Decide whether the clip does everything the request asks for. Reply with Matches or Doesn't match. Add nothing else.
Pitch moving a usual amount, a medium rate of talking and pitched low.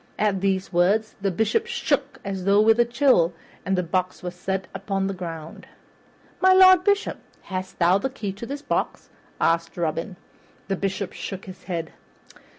Doesn't match